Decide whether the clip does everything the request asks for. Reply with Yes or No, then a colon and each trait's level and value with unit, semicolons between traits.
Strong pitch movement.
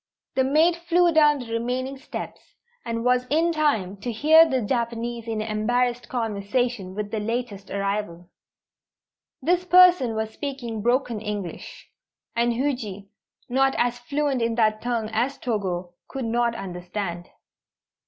No: average, 4.0 semitones